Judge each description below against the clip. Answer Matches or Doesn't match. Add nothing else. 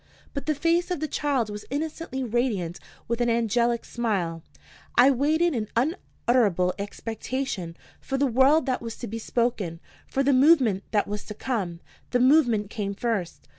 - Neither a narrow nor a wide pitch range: Matches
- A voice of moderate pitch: Doesn't match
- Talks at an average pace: Matches